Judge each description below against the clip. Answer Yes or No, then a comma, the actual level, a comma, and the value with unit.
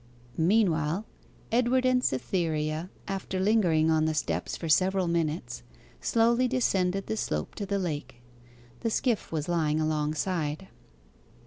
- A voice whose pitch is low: No, medium, 175 Hz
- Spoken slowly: Yes, slow, 125 wpm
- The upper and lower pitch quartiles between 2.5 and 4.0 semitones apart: No, average, 5.0 semitones